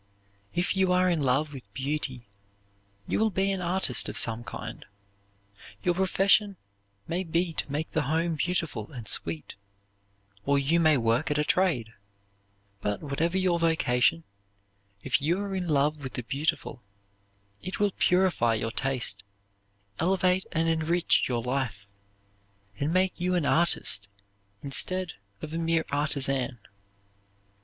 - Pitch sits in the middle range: Yes, medium, 160 Hz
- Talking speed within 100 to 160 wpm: Yes, average, 140 wpm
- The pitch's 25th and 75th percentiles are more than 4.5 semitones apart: Yes, average, 5.1 semitones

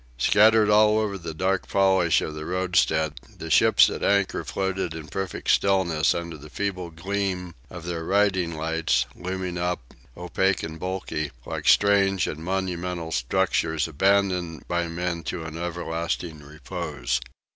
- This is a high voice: No, very low, 90 Hz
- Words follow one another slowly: No, average, 145 wpm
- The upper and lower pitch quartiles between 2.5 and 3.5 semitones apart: Yes, average, 2.9 semitones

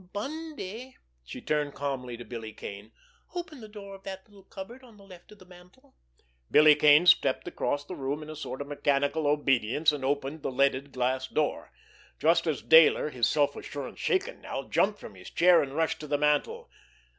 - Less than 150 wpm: No, average, 180 wpm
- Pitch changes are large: Yes, wide, 5.8 semitones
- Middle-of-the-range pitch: Yes, medium, 150 Hz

